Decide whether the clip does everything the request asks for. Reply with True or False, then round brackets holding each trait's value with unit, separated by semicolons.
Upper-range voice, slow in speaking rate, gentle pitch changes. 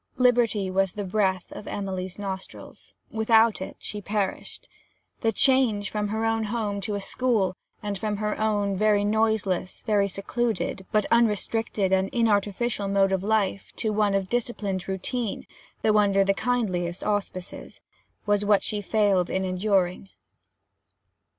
False (205 Hz; 145 wpm; 2.2 semitones)